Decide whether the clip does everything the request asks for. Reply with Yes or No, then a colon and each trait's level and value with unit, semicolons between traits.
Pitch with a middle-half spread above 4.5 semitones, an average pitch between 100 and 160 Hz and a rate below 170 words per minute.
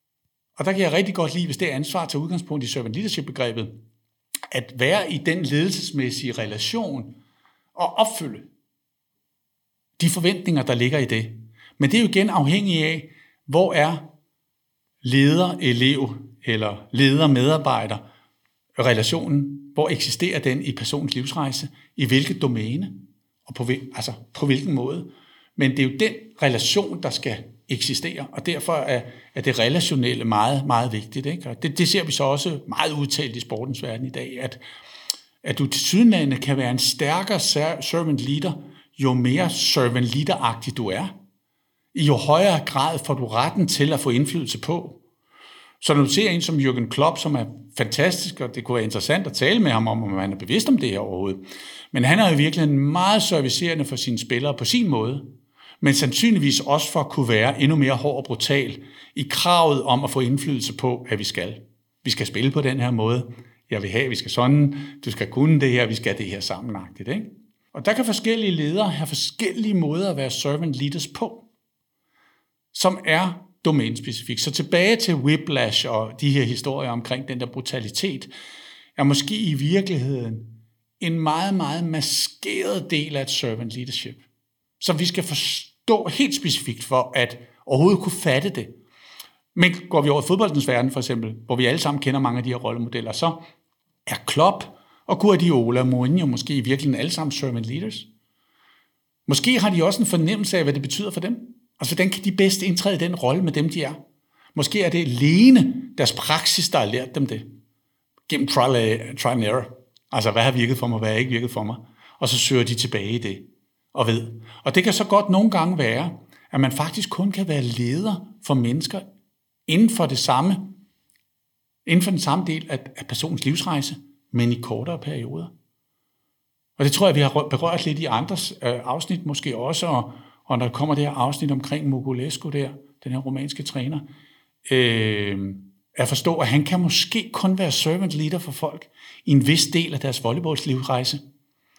No: average, 5.0 semitones; medium, 140 Hz; average, 190 wpm